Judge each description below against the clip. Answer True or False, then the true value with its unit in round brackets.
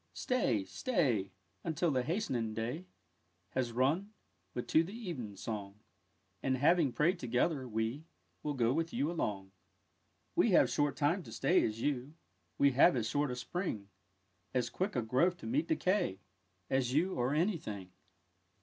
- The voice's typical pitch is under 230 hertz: True (135 Hz)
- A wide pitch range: True (6.8 semitones)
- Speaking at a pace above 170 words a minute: False (160 wpm)